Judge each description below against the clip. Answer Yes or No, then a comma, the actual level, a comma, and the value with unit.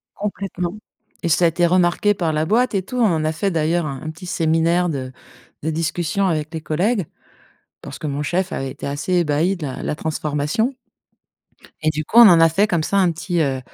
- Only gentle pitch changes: No, average, 3.2 semitones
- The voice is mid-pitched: Yes, medium, 165 Hz